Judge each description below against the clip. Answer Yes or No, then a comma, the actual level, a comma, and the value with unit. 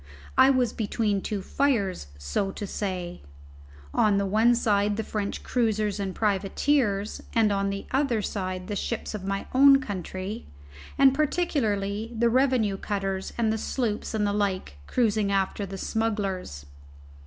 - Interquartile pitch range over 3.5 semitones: No, average, 2.9 semitones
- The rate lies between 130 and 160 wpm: Yes, average, 150 wpm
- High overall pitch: Yes, high, 210 Hz